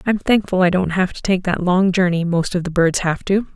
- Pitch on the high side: No, medium, 180 Hz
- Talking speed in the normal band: No, fast, 270 wpm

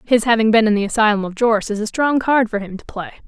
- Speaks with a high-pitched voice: Yes, high, 220 Hz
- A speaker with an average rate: No, fast, 295 wpm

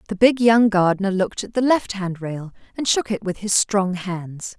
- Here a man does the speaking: No, female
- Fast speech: Yes, fast, 225 wpm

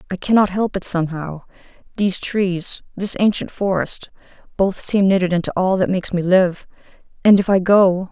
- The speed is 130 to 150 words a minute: No, average, 170 wpm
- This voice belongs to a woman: Yes, female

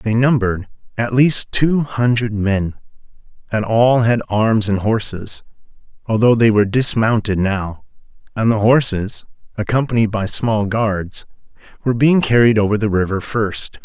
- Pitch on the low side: Yes, low, 110 Hz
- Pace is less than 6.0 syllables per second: Yes, 4.5 syllables/s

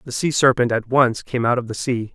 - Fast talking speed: Yes, fast, 280 wpm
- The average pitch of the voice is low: Yes, low, 125 Hz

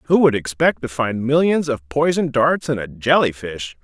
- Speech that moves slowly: No, fast, 205 wpm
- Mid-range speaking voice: No, low, 130 Hz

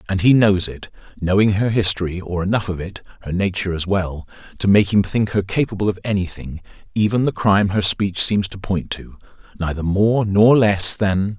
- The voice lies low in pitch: Yes, low, 100 Hz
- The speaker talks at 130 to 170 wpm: No, average, 185 wpm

